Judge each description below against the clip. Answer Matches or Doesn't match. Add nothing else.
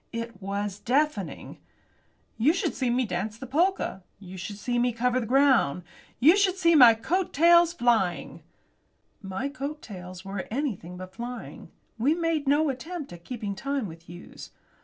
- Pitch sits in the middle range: Doesn't match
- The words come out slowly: Doesn't match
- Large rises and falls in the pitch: Matches